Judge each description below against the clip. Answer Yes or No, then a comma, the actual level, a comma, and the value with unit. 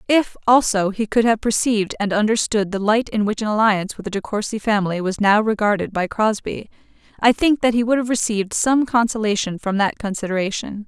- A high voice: Yes, high, 215 Hz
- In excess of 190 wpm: Yes, average, 200 wpm